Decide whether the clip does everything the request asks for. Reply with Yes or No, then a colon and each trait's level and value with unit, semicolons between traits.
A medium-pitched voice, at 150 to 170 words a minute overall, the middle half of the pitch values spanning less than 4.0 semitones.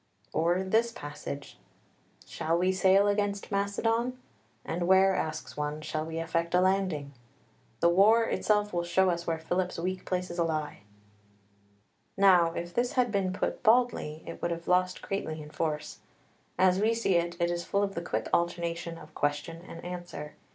Yes: medium, 175 Hz; average, 165 wpm; average, 2.9 semitones